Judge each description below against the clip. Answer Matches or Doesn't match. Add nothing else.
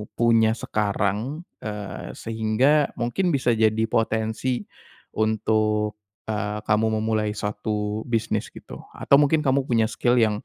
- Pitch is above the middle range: Doesn't match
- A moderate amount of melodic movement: Doesn't match